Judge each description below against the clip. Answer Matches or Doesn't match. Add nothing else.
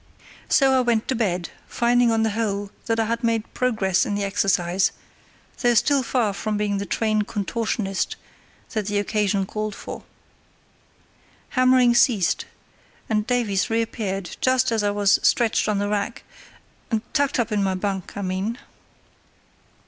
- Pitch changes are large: Doesn't match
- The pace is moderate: Matches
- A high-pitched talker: Matches